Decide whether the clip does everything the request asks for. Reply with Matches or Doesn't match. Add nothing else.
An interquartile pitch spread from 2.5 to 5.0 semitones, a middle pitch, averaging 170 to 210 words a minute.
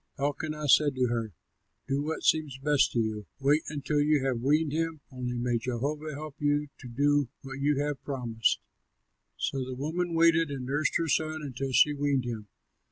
Matches